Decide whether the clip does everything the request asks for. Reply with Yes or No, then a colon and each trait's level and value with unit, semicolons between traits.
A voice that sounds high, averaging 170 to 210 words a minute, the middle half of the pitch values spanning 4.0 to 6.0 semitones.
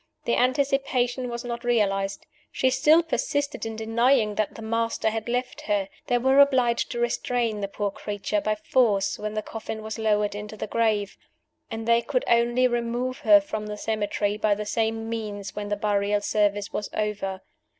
No: high, 225 Hz; average, 180 wpm; average, 2.7 semitones